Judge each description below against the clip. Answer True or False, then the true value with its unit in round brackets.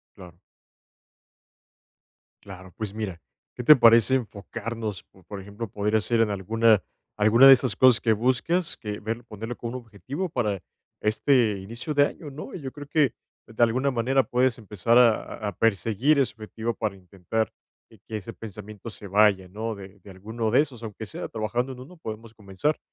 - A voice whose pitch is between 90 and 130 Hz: True (110 Hz)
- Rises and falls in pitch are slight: False (3.2 semitones)